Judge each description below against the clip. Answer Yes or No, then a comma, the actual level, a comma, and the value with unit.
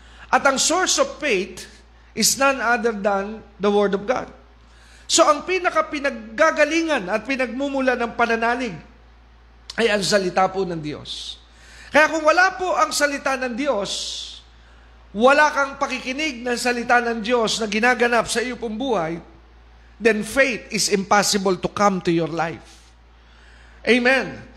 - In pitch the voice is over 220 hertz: Yes, high, 230 Hz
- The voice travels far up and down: Yes, wide, 7.0 semitones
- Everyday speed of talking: Yes, average, 140 wpm